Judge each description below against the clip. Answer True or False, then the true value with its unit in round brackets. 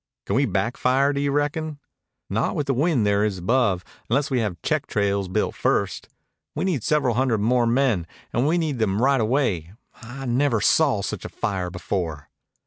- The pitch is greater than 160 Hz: False (120 Hz)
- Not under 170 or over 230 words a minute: True (190 wpm)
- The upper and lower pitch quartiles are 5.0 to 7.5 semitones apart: True (5.6 semitones)